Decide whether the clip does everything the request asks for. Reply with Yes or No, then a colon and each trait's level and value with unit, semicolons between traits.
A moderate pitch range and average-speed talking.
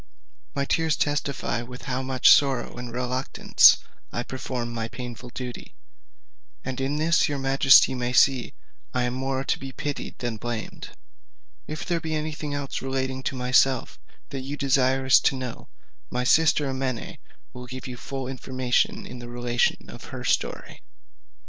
No: narrow, 1.7 semitones; average, 160 wpm